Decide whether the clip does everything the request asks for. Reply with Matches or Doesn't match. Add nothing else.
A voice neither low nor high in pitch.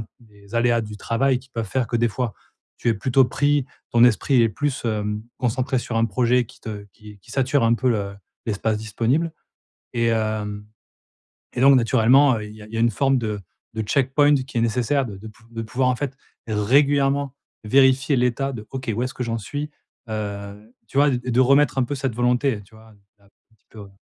Doesn't match